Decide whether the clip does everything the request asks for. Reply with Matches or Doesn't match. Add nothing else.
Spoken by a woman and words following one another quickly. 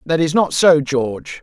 Doesn't match